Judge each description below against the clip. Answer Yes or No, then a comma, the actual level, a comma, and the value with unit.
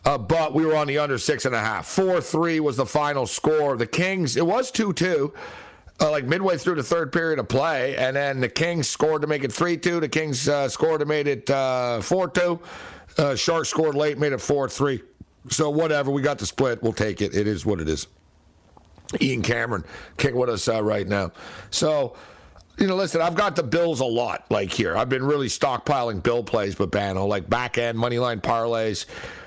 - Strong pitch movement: Yes, wide, 6.0 semitones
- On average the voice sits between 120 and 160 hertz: Yes, medium, 140 Hz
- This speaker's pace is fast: Yes, fast, 220 wpm